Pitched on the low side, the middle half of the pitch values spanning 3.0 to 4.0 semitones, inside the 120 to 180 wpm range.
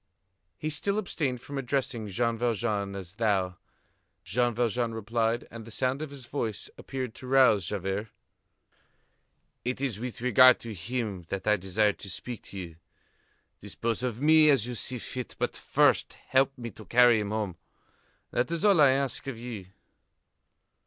Yes: low, 120 Hz; average, 3.5 semitones; average, 165 wpm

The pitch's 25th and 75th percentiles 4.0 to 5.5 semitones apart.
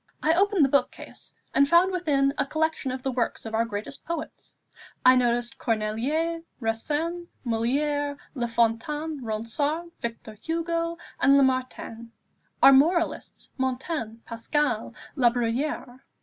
Yes: average, 5.2 semitones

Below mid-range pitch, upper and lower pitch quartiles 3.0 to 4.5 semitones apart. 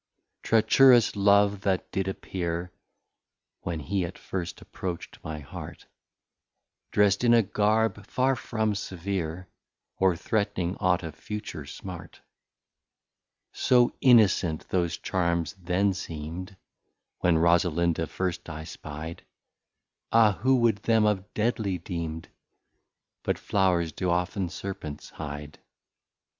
Yes: very low, 95 Hz; average, 3.5 semitones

